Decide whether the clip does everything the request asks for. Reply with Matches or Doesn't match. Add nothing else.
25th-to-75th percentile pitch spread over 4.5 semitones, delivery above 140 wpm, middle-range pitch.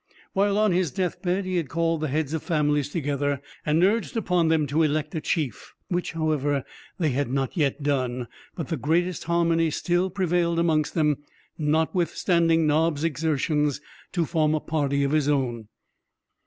Doesn't match